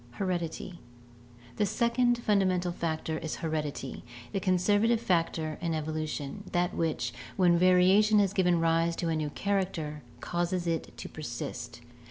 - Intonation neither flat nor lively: Yes, average, 3.4 semitones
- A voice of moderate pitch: Yes, medium, 170 Hz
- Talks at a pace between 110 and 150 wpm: Yes, average, 140 wpm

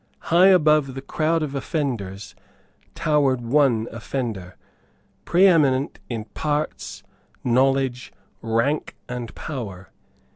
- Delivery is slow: Yes, slow, 95 wpm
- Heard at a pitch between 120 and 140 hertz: Yes, low, 135 Hz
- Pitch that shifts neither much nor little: Yes, average, 4.6 semitones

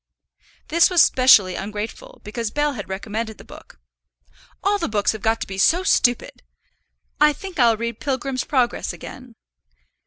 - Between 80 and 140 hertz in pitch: No, high, 240 Hz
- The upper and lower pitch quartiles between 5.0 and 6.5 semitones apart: Yes, wide, 5.5 semitones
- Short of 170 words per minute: Yes, average, 155 wpm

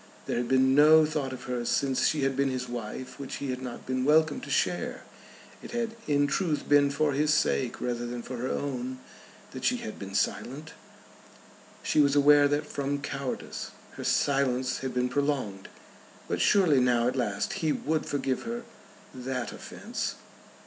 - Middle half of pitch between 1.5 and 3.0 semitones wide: Yes, narrow, 2.6 semitones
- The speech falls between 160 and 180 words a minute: Yes, average, 175 wpm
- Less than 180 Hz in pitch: Yes, low, 135 Hz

